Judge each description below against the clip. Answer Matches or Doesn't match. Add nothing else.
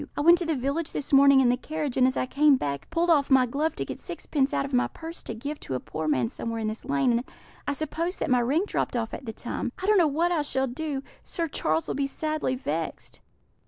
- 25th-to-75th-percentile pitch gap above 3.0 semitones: Matches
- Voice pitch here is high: Matches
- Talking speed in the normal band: Doesn't match